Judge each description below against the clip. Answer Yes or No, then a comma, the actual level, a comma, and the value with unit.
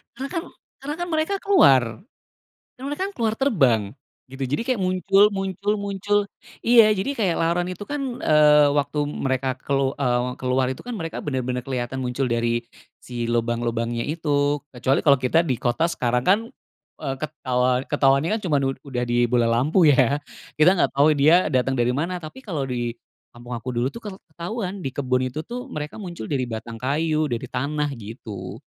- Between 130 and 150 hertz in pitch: Yes, medium, 140 Hz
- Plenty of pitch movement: Yes, wide, 6.2 semitones